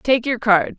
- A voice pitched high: Yes, high, 230 Hz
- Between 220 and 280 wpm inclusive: Yes, fast, 230 wpm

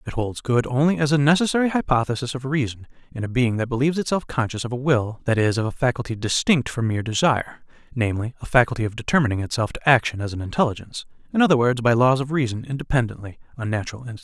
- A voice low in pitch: Yes, low, 125 Hz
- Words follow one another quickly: Yes, fast, 215 wpm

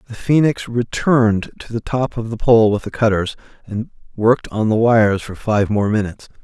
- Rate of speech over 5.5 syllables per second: No, 5.3 syllables/s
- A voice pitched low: Yes, low, 115 Hz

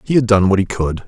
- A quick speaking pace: Yes, fast, 335 wpm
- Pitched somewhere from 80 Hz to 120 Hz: Yes, low, 105 Hz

